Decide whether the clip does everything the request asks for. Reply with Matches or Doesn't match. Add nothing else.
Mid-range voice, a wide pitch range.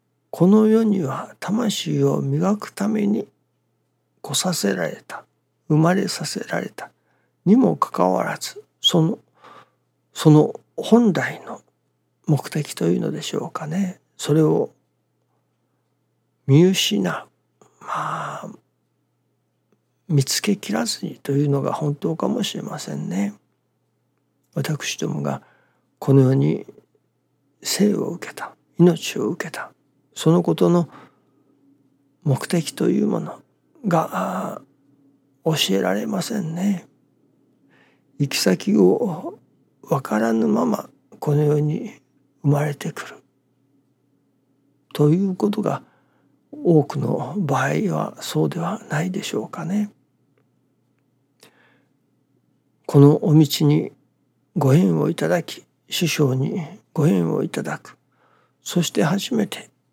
Doesn't match